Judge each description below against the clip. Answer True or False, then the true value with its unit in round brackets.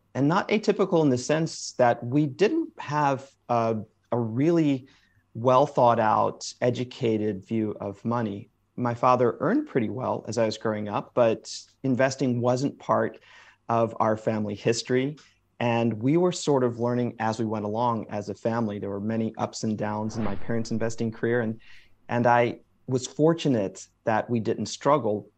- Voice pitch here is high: False (115 Hz)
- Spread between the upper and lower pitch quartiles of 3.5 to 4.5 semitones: False (3.1 semitones)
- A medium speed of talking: True (170 wpm)